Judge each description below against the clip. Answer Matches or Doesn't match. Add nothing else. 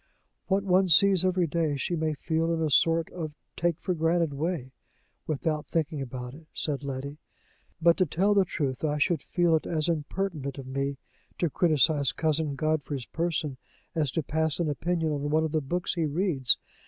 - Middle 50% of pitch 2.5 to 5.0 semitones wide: Matches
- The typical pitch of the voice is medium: Matches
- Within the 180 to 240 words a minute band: Matches